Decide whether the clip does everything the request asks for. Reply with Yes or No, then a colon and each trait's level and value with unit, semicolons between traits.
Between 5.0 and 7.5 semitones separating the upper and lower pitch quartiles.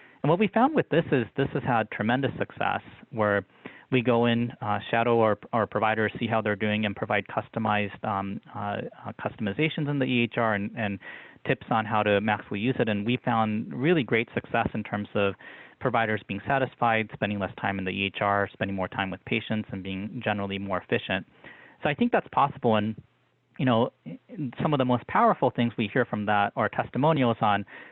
No: average, 3.3 semitones